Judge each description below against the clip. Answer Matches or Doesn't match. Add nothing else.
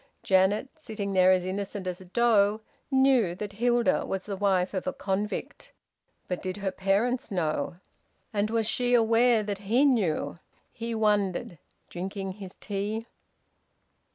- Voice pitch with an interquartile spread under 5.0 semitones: Matches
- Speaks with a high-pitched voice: Matches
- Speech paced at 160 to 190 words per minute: Doesn't match